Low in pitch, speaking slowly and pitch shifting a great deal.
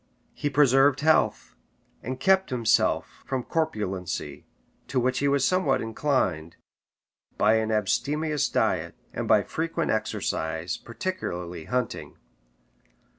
Yes: low, 130 Hz; slow, 110 wpm; wide, 5.7 semitones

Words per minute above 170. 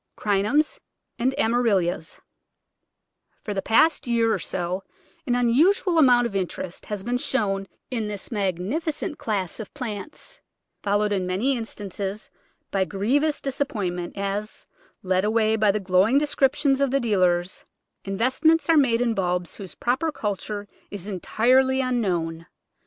No: average, 140 wpm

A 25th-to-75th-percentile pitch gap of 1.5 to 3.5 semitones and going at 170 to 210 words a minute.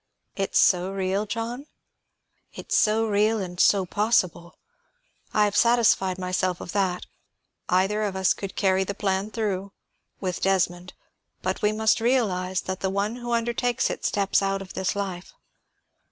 No: narrow, 2.4 semitones; average, 155 wpm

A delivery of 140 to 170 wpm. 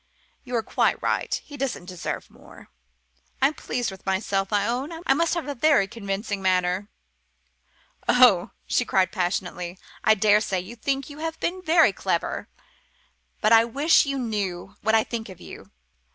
Yes: average, 160 wpm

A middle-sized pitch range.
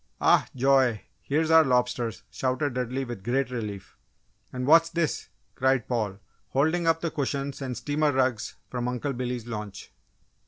Yes: average, 3.0 semitones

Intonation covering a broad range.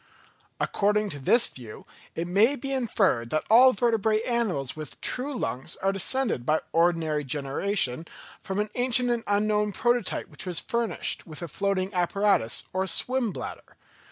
Yes: wide, 6.2 semitones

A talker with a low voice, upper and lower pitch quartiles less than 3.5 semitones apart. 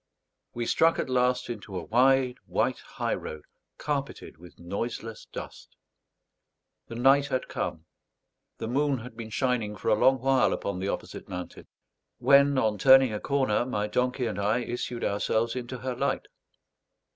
No: low, 120 Hz; average, 3.8 semitones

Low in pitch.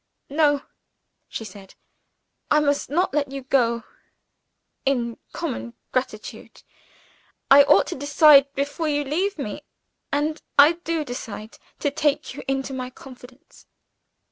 No: very high, 280 Hz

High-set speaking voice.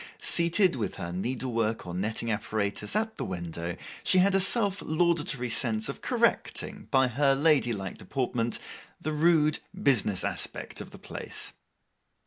No: low, 125 Hz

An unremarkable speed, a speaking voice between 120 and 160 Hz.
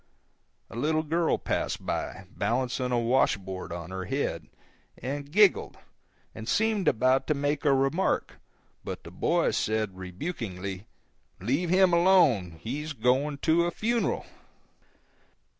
No: slow, 130 wpm; low, 135 Hz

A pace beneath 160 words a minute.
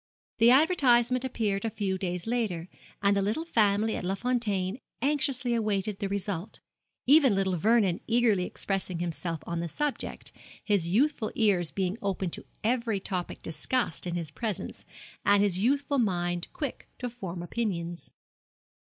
Yes: average, 150 wpm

